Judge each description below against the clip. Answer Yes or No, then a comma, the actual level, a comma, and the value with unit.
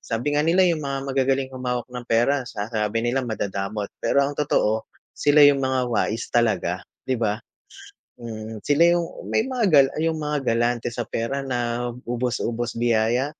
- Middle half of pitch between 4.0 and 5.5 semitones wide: No, average, 3.5 semitones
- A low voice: Yes, low, 120 Hz